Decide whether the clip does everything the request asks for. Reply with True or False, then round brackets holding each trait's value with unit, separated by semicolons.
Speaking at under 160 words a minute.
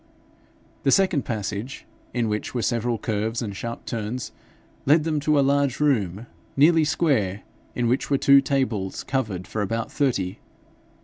True (150 wpm)